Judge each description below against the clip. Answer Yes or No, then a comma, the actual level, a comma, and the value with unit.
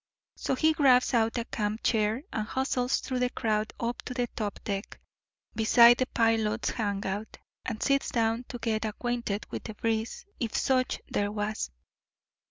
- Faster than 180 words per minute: No, average, 165 wpm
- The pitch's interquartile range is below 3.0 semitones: Yes, narrow, 2.5 semitones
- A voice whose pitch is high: Yes, high, 230 Hz